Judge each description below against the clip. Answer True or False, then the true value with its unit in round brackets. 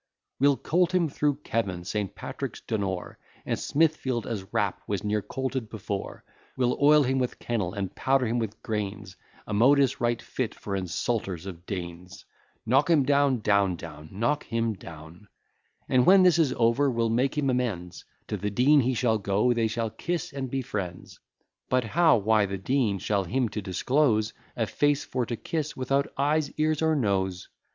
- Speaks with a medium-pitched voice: False (115 Hz)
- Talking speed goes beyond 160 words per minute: True (170 wpm)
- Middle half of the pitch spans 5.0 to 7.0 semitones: True (5.5 semitones)